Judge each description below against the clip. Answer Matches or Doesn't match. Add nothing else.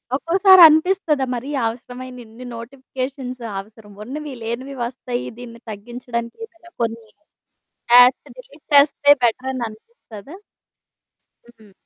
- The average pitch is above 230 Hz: Matches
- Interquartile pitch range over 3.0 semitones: Matches